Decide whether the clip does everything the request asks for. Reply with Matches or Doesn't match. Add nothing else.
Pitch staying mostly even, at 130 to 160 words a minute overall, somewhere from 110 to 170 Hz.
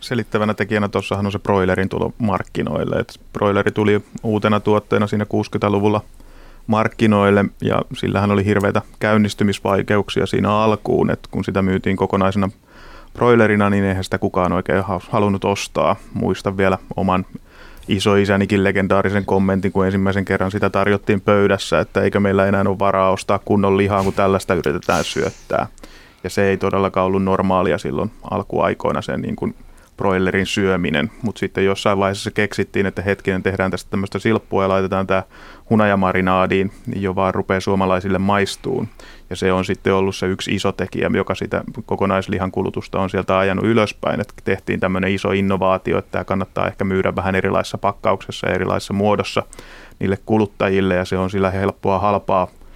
Doesn't match